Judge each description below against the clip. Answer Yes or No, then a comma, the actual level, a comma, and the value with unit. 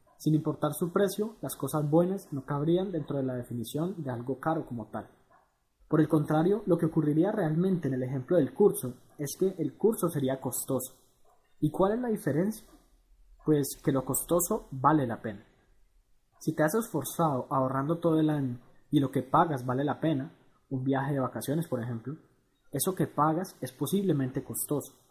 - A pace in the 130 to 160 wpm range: No, average, 180 wpm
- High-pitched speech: No, medium, 145 Hz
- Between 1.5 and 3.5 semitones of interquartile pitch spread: No, average, 4.1 semitones